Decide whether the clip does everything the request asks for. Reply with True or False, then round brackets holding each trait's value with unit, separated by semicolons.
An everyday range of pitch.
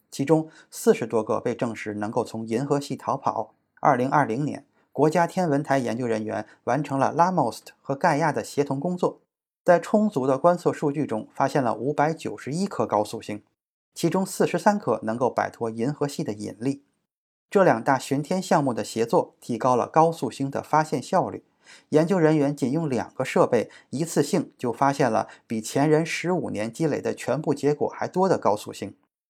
False (5.7 semitones)